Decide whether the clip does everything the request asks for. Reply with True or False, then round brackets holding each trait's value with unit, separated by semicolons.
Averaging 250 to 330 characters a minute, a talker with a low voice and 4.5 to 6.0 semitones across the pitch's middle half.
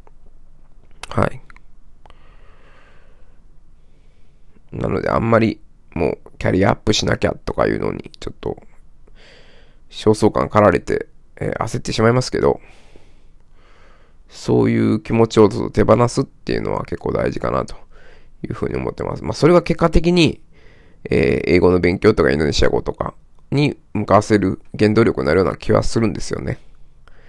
False (300 characters per minute; 95 Hz; 6.4 semitones)